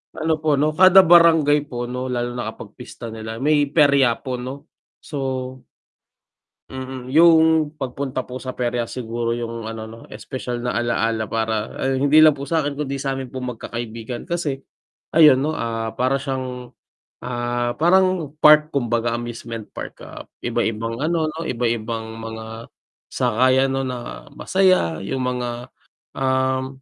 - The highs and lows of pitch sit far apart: No, average, 3.7 semitones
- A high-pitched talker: No, low, 130 Hz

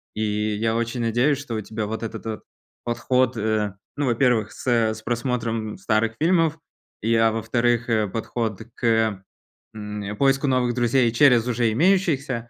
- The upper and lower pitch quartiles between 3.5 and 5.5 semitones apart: No, narrow, 2.5 semitones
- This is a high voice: No, low, 115 Hz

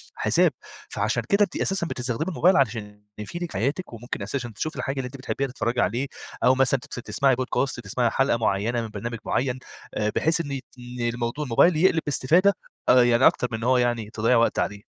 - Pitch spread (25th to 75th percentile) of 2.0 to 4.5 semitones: Yes, average, 3.0 semitones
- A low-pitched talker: Yes, low, 125 Hz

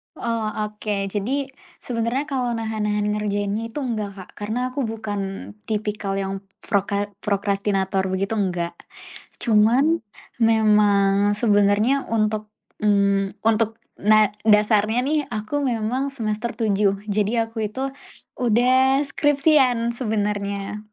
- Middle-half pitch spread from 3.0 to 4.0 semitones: No, narrow, 2.6 semitones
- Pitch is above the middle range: Yes, high, 215 Hz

